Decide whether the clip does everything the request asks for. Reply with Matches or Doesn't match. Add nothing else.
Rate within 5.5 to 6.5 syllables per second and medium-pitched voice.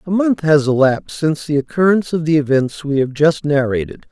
Matches